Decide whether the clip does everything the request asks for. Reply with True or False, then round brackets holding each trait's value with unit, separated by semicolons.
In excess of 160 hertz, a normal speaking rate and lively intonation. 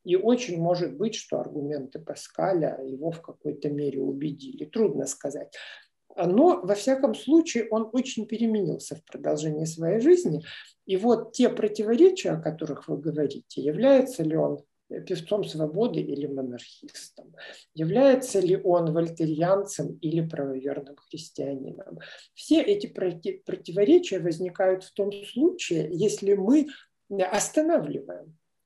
True (185 Hz; 120 wpm; 6.9 semitones)